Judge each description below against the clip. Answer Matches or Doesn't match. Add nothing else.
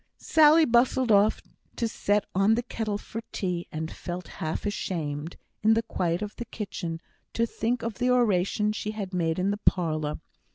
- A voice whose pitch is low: Doesn't match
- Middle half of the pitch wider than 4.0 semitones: Matches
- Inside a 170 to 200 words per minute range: Matches